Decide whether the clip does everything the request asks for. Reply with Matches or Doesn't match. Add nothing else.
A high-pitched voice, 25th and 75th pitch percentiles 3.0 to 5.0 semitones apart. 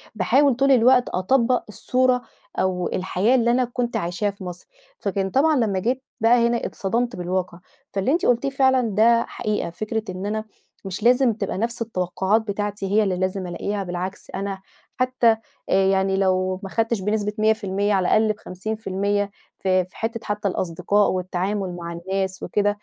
Matches